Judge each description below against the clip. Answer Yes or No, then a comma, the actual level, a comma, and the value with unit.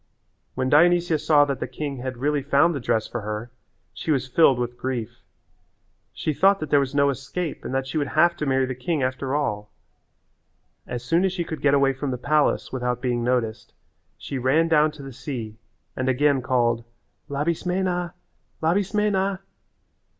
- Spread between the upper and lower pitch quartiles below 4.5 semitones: Yes, average, 4.0 semitones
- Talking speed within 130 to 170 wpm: No, average, 180 wpm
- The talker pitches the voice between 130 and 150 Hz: Yes, medium, 140 Hz